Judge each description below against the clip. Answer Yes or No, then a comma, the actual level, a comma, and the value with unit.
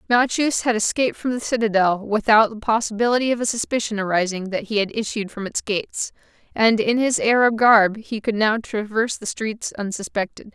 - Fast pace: No, average, 180 wpm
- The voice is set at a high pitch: Yes, high, 220 Hz